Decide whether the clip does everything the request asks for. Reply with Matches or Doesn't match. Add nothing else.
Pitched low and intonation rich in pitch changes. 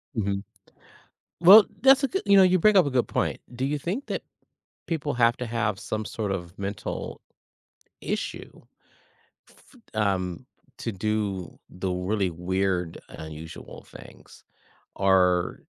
Matches